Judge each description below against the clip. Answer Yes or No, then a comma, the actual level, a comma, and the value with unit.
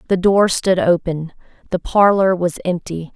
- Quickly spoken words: No, average, 150 wpm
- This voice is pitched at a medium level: Yes, medium, 180 Hz